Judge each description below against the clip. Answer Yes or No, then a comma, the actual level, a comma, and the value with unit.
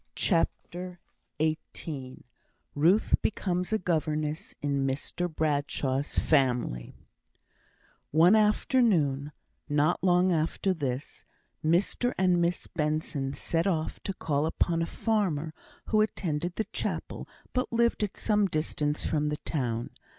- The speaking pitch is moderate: Yes, medium, 160 Hz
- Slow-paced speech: Yes, slow, 115 wpm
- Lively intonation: No, average, 3.9 semitones